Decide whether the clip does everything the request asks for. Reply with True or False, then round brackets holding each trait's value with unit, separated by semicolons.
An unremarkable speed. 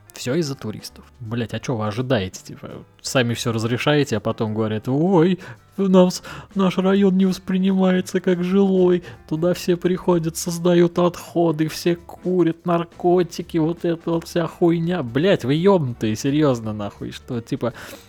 True (145 wpm)